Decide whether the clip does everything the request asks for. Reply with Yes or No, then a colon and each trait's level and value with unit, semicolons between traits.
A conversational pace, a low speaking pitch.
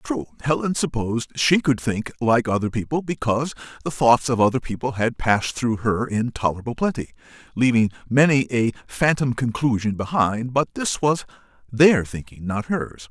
Yes: average, 155 wpm; low, 125 Hz